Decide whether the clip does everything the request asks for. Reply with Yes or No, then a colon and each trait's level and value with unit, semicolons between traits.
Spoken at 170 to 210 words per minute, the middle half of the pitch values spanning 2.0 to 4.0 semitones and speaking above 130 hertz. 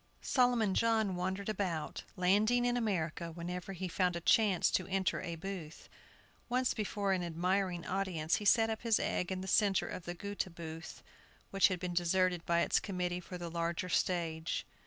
Yes: average, 180 wpm; average, 2.7 semitones; medium, 185 Hz